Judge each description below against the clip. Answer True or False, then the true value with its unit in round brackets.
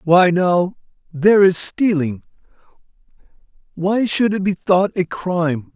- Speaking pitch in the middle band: True (180 Hz)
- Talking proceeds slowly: True (125 wpm)